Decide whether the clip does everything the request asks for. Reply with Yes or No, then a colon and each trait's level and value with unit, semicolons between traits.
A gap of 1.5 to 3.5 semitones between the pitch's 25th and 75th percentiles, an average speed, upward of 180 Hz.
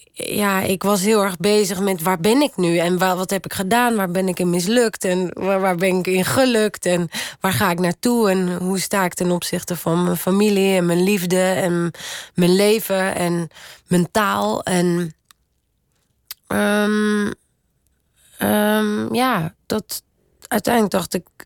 Yes: average, 2.7 semitones; average, 160 wpm; high, 190 Hz